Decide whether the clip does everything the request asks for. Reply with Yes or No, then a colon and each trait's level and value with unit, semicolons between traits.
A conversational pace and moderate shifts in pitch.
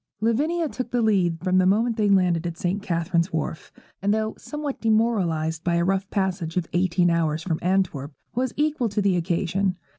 Yes: average, 185 wpm; average, 4.4 semitones